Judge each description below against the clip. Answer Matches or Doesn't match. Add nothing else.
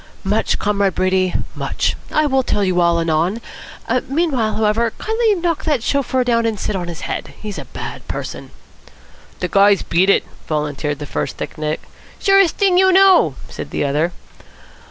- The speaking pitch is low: Doesn't match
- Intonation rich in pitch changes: Matches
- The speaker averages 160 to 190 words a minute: Matches